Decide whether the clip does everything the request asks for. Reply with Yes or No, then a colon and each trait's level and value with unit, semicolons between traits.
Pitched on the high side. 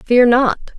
Yes: high, 245 Hz